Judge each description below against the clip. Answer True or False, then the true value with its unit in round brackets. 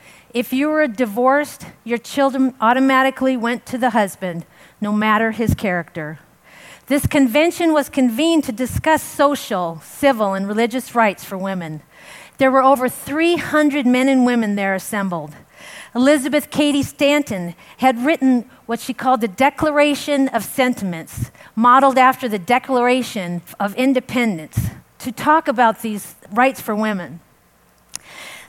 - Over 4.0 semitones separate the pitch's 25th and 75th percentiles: True (5.2 semitones)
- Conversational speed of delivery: False (130 wpm)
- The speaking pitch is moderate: False (250 Hz)